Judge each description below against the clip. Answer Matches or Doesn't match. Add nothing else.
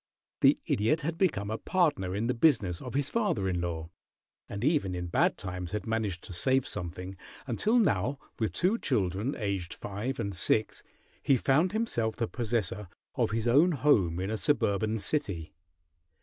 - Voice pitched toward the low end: Matches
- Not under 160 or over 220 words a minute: Matches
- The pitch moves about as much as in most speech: Doesn't match